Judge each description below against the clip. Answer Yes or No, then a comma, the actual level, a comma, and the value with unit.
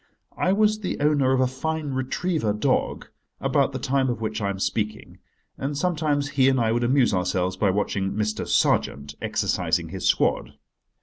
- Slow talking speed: No, average, 175 wpm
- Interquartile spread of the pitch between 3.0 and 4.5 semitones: No, wide, 5.5 semitones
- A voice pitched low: Yes, low, 130 Hz